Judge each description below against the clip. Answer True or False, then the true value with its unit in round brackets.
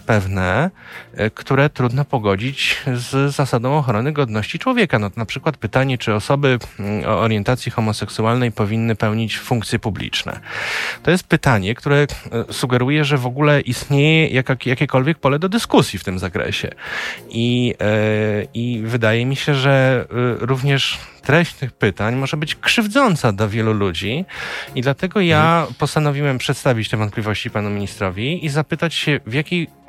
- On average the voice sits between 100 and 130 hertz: True (125 Hz)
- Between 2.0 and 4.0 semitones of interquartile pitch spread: False (4.9 semitones)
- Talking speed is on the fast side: False (140 wpm)